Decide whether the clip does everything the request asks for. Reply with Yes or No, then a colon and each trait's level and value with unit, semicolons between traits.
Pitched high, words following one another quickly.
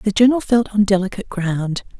No: high, 205 Hz; average, 180 wpm